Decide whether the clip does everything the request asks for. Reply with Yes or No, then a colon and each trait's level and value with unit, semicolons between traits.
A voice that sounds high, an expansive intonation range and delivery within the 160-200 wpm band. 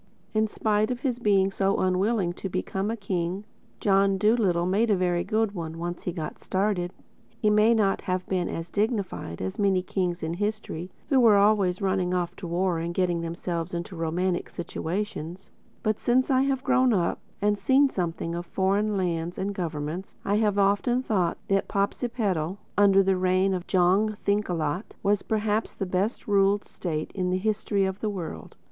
No: high, 195 Hz; average, 3.0 semitones; average, 175 wpm